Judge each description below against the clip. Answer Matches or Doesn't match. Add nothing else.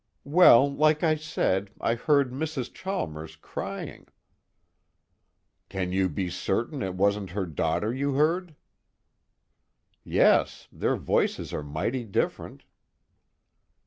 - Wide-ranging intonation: Matches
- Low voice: Matches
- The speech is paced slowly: Matches